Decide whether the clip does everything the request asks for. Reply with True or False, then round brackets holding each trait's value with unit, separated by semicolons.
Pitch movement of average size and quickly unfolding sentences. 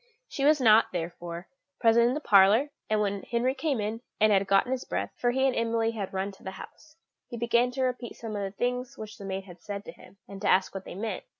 True (3.9 semitones; 255 wpm)